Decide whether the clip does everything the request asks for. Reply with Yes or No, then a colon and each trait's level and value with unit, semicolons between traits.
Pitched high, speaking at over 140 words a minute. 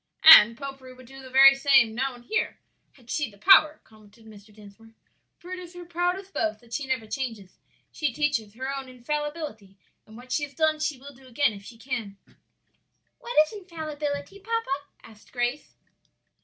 Yes: very high, 265 Hz; average, 180 wpm